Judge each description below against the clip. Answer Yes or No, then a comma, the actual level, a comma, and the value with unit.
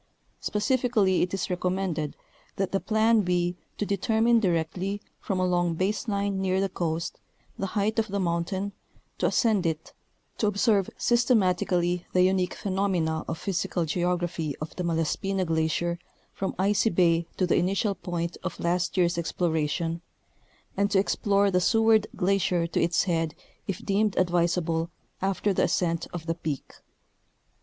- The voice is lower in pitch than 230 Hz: Yes, medium, 185 Hz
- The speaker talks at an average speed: Yes, average, 150 wpm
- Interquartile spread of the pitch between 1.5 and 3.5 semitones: Yes, average, 2.8 semitones